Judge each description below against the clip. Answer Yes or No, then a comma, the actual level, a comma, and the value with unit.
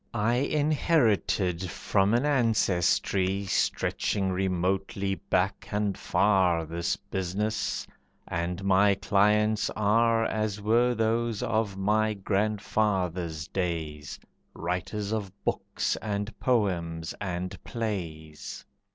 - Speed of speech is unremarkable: No, slow, 95 wpm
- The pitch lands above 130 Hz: No, low, 100 Hz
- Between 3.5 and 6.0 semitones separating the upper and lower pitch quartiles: No, average, 3.0 semitones